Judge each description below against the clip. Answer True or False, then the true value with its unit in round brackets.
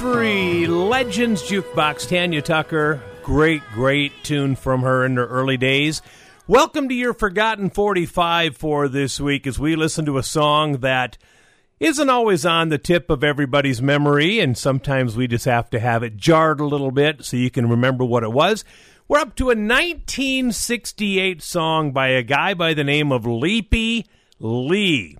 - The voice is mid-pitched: True (150 Hz)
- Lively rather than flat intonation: True (5.9 semitones)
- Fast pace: False (170 wpm)